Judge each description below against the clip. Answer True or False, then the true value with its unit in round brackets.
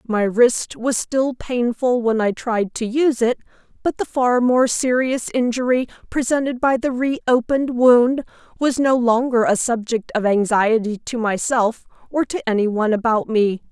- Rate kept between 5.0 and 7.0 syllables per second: False (4.5 syllables/s)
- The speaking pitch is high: True (240 Hz)